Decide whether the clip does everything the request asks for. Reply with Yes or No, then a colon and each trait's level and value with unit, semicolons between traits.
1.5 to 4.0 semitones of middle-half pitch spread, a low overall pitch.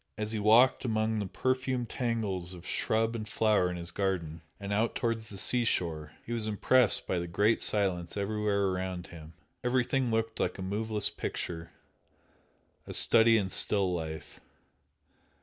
Yes: average, 3.7 semitones; low, 105 Hz